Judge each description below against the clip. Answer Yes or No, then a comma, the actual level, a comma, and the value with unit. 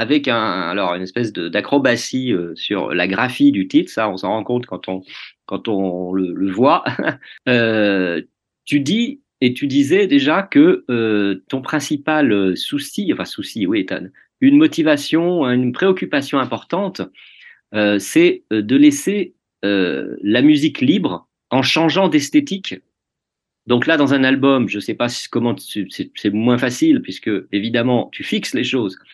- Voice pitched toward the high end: No, medium, 140 Hz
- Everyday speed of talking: Yes, average, 155 wpm